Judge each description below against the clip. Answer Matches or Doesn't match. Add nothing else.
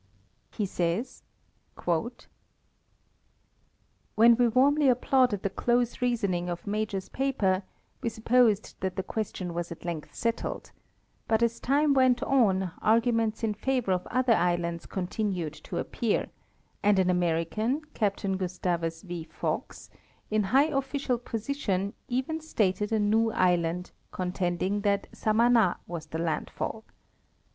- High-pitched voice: Matches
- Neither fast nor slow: Doesn't match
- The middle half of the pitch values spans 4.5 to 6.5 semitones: Matches